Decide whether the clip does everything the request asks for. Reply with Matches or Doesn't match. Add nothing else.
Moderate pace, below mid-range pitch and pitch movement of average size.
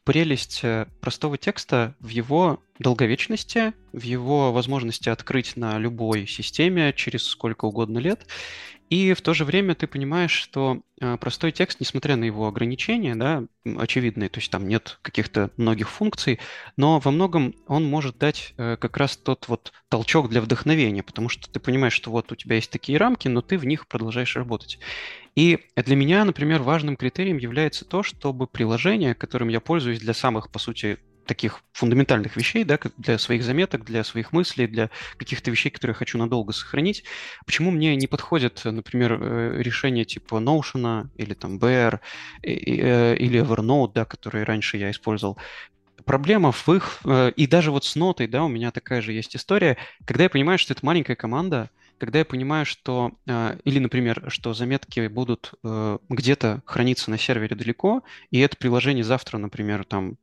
Doesn't match